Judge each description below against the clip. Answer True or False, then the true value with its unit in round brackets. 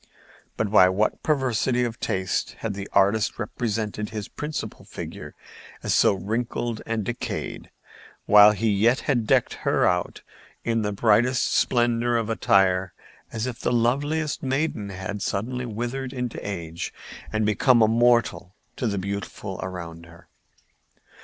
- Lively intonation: False (3.4 semitones)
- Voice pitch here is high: False (110 Hz)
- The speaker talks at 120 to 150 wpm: True (140 wpm)